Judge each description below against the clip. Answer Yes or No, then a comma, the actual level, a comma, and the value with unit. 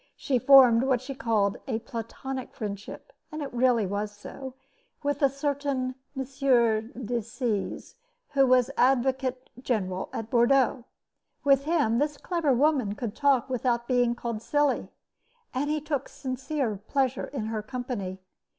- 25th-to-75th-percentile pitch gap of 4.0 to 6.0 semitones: No, average, 3.1 semitones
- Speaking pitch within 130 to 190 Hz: No, very high, 255 Hz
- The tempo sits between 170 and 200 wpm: No, average, 140 wpm